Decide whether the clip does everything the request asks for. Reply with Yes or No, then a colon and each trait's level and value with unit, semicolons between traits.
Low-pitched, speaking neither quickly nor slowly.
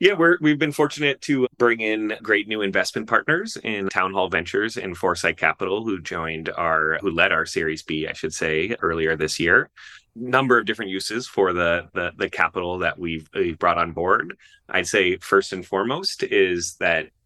Yes: low, 110 Hz; average, 190 wpm